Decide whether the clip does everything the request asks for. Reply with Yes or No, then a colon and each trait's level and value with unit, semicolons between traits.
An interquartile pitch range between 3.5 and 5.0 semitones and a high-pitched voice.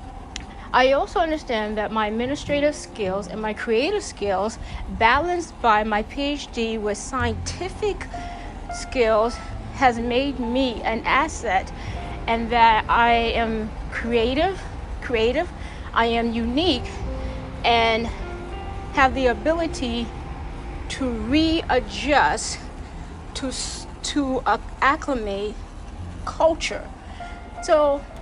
Yes: average, 4.6 semitones; high, 235 Hz